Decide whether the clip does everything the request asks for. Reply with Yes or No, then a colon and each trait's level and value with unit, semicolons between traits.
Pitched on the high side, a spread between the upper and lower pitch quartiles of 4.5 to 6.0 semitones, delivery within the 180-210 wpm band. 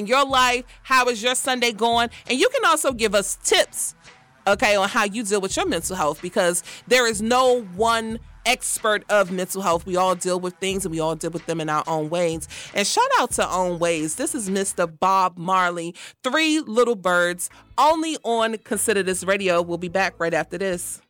Yes: high, 195 Hz; wide, 5.5 semitones; fast, 205 wpm